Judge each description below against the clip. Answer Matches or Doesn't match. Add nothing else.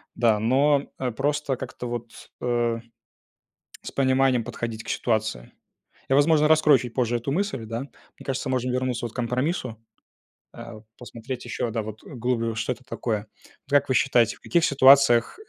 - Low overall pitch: Matches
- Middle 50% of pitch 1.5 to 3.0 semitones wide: Matches